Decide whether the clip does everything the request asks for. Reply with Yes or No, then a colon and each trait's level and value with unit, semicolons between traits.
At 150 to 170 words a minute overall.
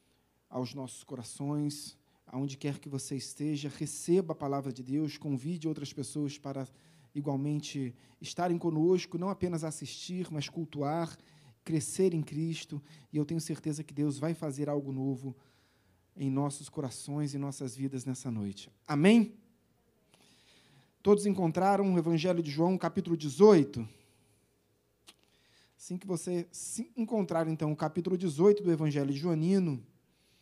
No: average, 135 wpm